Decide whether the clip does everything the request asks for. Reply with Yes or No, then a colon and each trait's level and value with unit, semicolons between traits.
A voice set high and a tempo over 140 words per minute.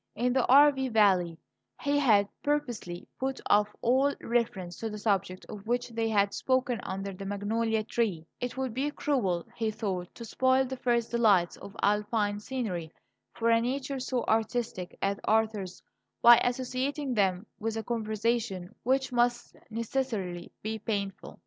Yes: high, 225 Hz; average, 155 wpm